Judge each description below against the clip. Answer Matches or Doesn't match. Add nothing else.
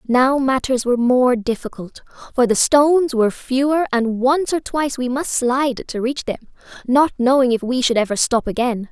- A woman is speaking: Matches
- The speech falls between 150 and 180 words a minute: Doesn't match